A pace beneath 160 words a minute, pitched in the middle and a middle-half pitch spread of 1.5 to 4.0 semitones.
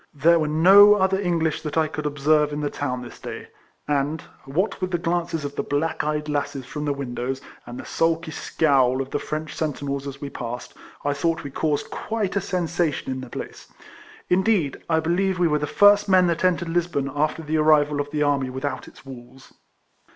No: average, 200 wpm; medium, 150 Hz; average, 3.2 semitones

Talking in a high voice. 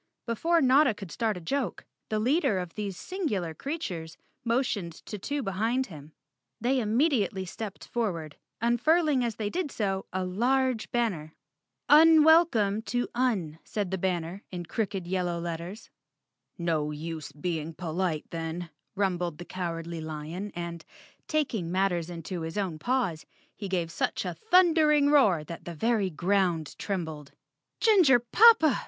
Yes: high, 195 Hz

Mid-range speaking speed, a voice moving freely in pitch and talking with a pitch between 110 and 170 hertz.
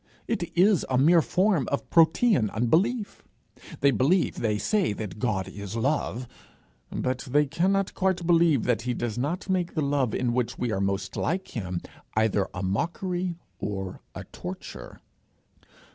Yes: average, 155 wpm; wide, 8.2 semitones; medium, 140 Hz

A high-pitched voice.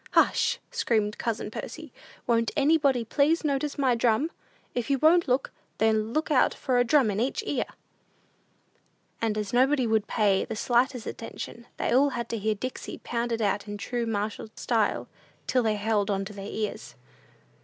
Yes: high, 235 Hz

